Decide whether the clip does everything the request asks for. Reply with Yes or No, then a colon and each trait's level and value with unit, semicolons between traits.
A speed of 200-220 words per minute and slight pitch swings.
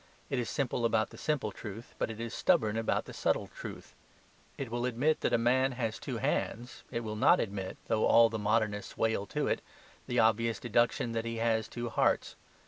Yes: fast, 205 wpm; narrow, 1.7 semitones